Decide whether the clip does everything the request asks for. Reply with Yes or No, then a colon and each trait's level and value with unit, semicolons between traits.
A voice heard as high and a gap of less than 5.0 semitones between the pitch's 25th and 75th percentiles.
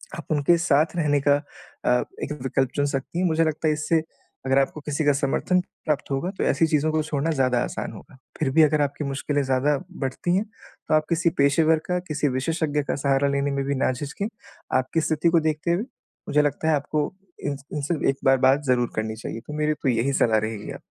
No: medium, 145 Hz; narrow, 2.6 semitones